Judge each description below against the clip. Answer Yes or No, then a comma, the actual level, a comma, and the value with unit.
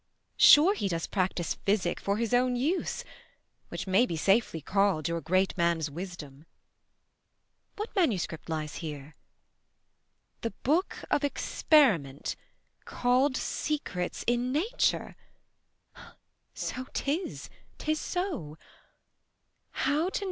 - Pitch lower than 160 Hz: No, high, 205 Hz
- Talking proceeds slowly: Yes, slow, 105 wpm